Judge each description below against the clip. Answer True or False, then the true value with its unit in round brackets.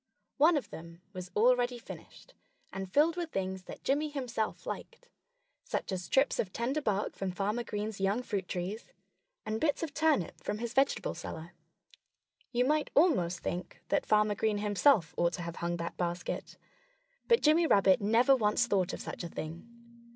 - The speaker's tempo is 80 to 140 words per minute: False (175 wpm)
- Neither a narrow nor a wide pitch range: False (6.7 semitones)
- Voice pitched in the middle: False (210 Hz)